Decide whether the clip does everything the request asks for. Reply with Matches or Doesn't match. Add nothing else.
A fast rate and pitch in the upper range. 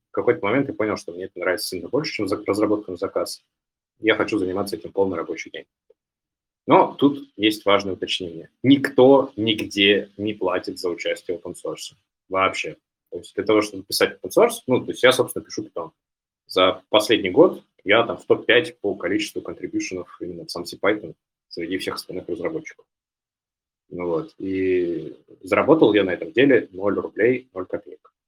Matches